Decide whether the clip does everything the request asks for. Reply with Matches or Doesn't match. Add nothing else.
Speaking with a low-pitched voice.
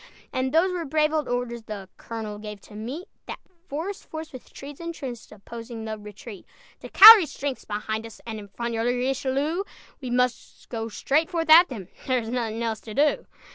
Doesn't match